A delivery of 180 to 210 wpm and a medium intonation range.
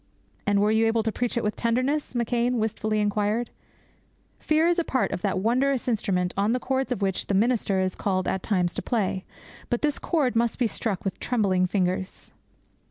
Yes: average, 195 wpm; average, 3.9 semitones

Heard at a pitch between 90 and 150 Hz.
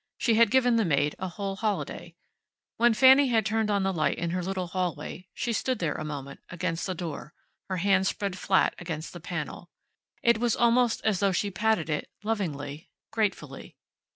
No: high, 190 Hz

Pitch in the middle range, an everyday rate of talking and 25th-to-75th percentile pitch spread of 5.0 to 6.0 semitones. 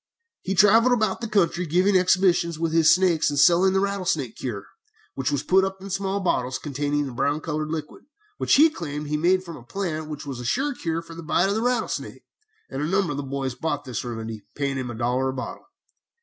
No: medium, 160 Hz; fast, 225 wpm; wide, 5.5 semitones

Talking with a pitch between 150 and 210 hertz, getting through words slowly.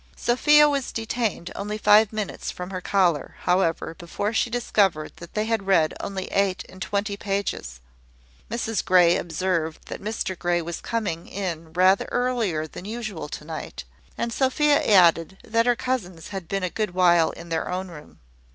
No: high, 190 Hz; average, 170 wpm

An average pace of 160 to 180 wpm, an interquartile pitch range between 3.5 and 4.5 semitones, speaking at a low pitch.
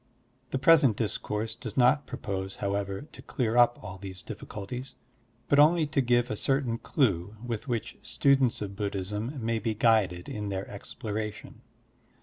No: average, 150 wpm; average, 3.9 semitones; low, 110 Hz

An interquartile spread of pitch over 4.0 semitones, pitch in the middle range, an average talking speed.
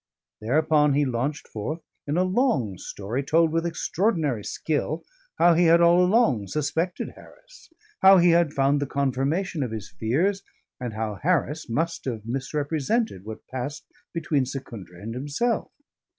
Yes: wide, 5.4 semitones; medium, 145 Hz; average, 150 wpm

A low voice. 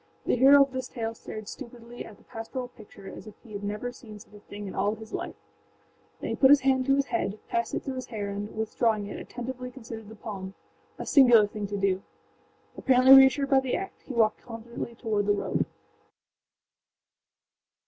No: high, 230 Hz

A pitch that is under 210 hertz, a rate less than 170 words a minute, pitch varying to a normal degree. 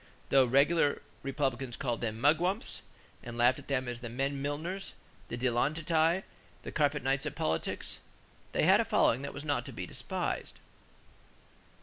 Yes: medium, 140 Hz; average, 160 wpm; average, 3.6 semitones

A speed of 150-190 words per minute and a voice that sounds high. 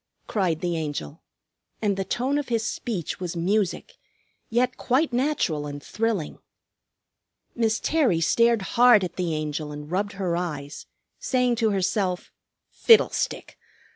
No: slow, 135 wpm; high, 195 Hz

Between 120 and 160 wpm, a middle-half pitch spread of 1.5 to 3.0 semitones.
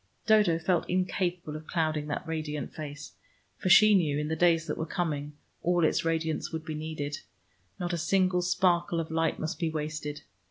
No: average, 185 wpm; narrow, 2.4 semitones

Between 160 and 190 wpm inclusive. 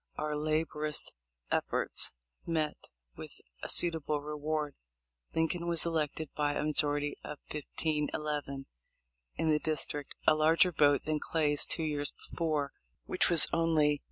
No: average, 140 wpm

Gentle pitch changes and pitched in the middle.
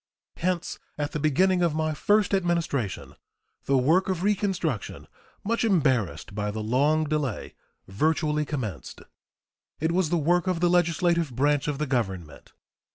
No: average, 5.0 semitones; medium, 155 Hz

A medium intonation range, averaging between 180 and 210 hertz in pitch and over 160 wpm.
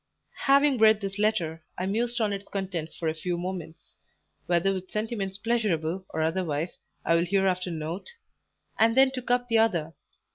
Yes: average, 4.7 semitones; high, 190 Hz; average, 170 wpm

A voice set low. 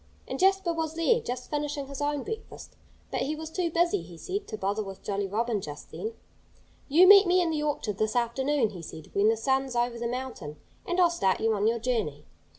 No: very high, 265 Hz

